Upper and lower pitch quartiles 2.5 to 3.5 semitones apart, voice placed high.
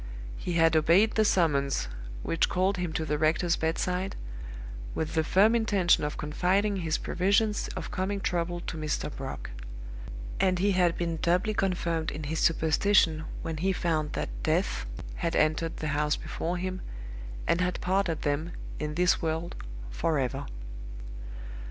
No: average, 3.1 semitones; medium, 170 Hz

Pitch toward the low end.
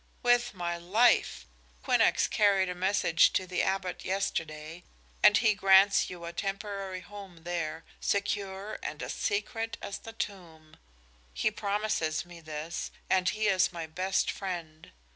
No: high, 190 Hz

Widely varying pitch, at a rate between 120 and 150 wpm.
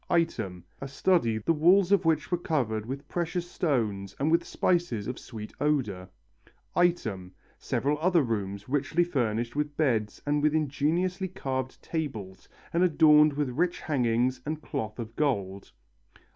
Yes: wide, 6.5 semitones; average, 145 wpm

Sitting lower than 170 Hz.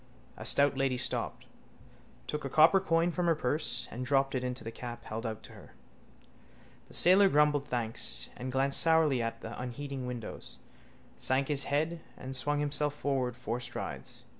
Yes: low, 135 Hz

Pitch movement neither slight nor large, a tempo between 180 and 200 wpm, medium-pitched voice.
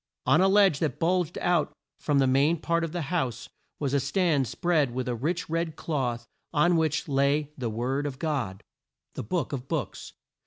Yes: average, 4.2 semitones; average, 190 wpm; medium, 150 Hz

